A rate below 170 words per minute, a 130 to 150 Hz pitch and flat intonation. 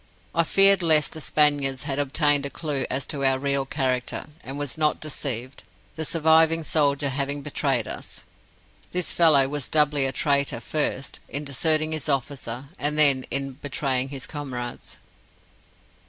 Yes: average, 155 wpm; medium, 140 Hz; narrow, 2.2 semitones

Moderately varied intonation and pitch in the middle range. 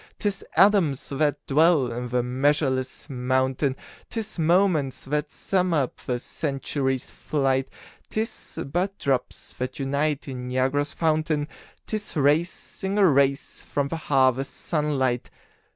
Yes: average, 3.6 semitones; medium, 145 Hz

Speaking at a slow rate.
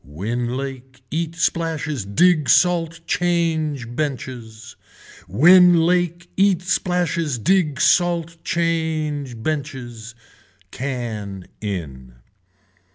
Yes: slow, 85 wpm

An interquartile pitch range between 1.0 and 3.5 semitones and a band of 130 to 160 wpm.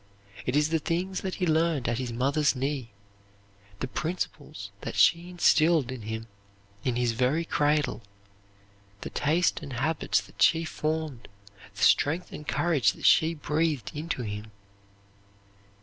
No: average, 4.5 semitones; average, 145 wpm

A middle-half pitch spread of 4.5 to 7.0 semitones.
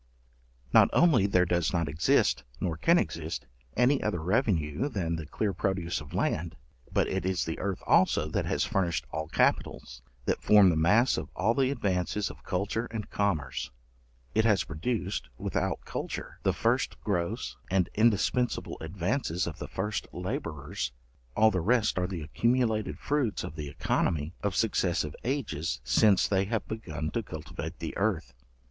Yes: average, 5.2 semitones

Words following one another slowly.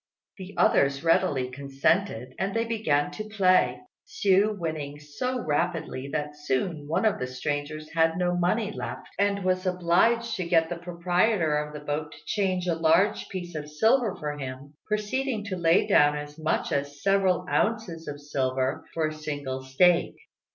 No: average, 165 wpm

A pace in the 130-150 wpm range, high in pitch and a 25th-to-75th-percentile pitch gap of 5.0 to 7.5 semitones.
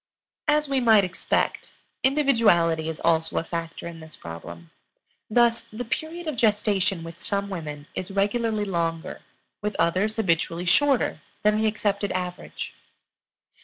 Yes: slow, 135 wpm; high, 200 Hz; average, 5.3 semitones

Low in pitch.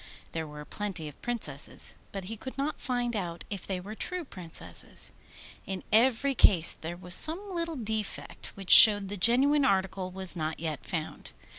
No: high, 200 Hz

